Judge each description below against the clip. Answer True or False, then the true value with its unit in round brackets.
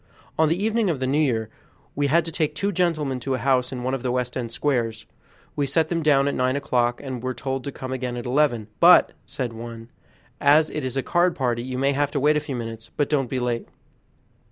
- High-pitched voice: False (135 Hz)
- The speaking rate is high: True (245 wpm)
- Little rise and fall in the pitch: False (3.3 semitones)